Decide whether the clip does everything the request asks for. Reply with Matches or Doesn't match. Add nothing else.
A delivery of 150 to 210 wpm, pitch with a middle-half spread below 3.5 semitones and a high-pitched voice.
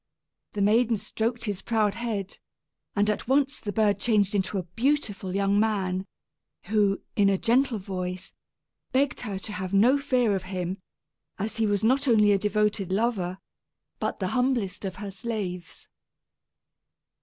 Matches